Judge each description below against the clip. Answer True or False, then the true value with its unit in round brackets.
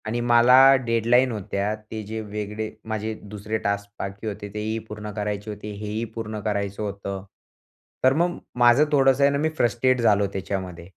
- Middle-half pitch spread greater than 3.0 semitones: False (2.7 semitones)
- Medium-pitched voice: False (110 Hz)